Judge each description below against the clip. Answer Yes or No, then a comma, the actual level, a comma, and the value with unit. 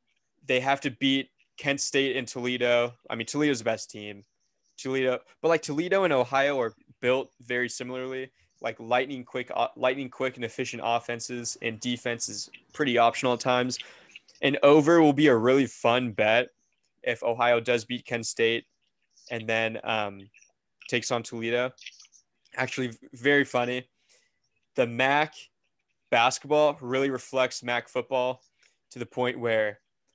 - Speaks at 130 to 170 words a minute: Yes, average, 145 wpm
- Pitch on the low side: Yes, low, 125 Hz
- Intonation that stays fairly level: Yes, narrow, 2.1 semitones